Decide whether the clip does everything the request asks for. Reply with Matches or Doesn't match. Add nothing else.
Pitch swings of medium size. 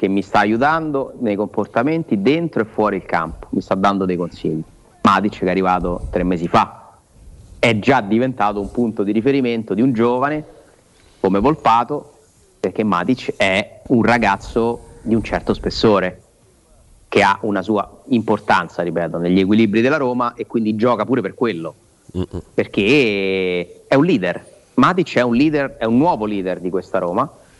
Matches